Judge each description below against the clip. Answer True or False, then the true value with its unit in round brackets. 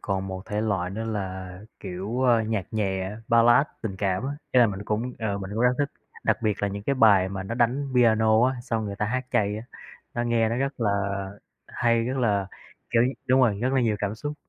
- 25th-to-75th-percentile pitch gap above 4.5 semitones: False (3.3 semitones)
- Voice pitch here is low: True (110 Hz)